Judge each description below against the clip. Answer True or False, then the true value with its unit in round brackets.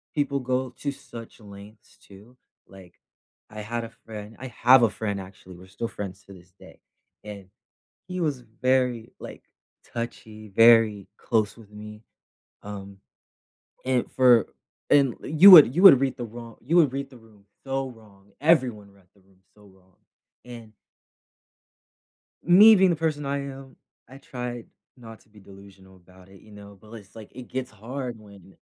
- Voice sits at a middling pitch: False (115 Hz)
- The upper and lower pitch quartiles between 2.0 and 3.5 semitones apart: False (4.4 semitones)